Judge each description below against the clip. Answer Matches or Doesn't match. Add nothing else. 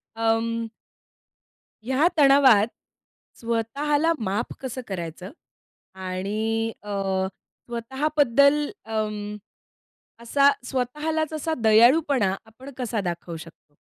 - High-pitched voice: Matches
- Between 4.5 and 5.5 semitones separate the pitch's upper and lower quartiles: Matches